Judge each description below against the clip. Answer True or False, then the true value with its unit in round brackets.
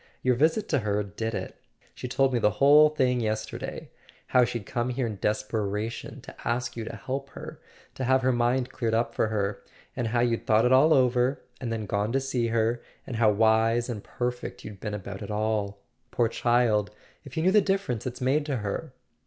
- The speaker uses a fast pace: True (210 wpm)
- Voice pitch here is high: False (120 Hz)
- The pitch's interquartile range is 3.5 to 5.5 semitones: False (3.0 semitones)